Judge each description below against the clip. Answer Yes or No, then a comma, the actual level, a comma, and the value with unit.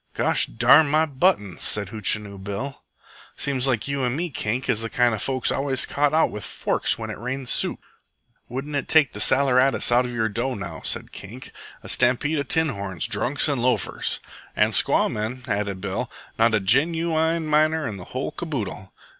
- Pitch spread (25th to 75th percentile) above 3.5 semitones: Yes, average, 5.1 semitones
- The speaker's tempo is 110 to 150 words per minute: No, average, 190 wpm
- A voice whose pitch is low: Yes, low, 125 Hz